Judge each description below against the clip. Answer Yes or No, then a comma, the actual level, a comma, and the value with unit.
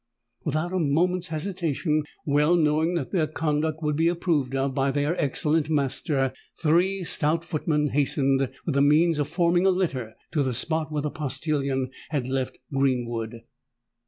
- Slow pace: No, average, 150 wpm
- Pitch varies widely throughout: No, average, 3.2 semitones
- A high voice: No, medium, 150 Hz